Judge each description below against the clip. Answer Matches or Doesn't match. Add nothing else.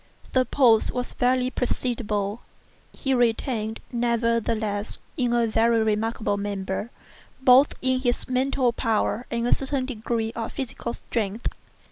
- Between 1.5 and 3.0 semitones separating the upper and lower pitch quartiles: Matches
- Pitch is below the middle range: Doesn't match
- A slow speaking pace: Matches